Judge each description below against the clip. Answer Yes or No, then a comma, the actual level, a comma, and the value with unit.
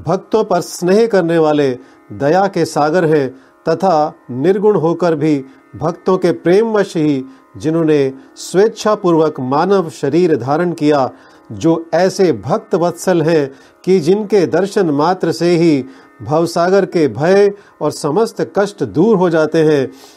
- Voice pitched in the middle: Yes, medium, 165 Hz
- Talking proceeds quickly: No, average, 130 wpm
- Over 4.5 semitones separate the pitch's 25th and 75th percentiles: No, average, 4.0 semitones